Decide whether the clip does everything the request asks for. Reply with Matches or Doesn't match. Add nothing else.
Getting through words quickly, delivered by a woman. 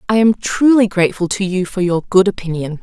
Matches